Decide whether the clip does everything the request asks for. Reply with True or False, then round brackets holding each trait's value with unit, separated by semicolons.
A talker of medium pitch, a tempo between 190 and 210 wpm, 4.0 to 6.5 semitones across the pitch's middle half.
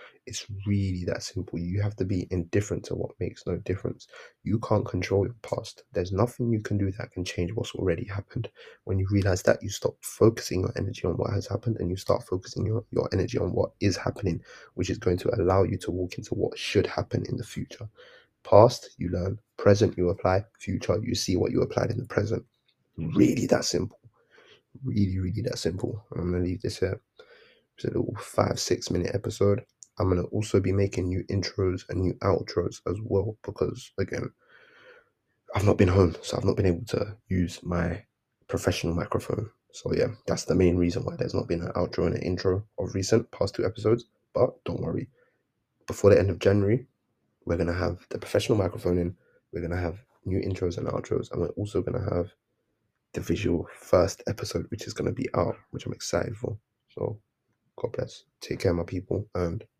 False (100 Hz; 200 wpm; 4.4 semitones)